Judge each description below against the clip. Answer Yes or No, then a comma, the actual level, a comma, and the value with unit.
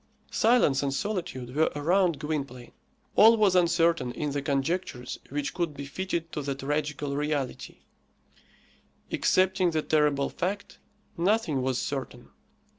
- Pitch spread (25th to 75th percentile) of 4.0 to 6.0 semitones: Yes, average, 4.4 semitones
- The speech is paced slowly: Yes, slow, 125 wpm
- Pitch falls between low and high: Yes, medium, 150 Hz